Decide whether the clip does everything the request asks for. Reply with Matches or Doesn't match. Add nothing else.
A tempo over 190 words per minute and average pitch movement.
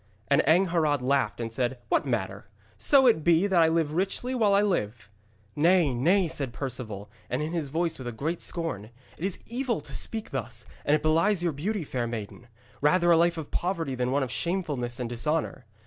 Doesn't match